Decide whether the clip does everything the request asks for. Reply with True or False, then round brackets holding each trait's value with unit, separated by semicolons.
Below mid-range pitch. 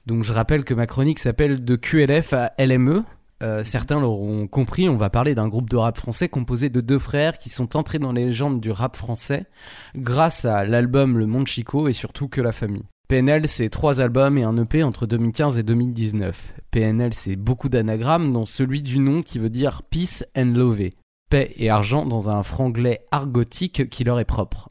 True (125 Hz)